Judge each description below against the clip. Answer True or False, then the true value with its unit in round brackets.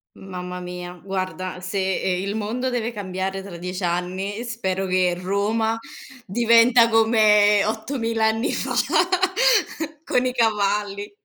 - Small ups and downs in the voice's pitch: False (3.3 semitones)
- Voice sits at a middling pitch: False (205 Hz)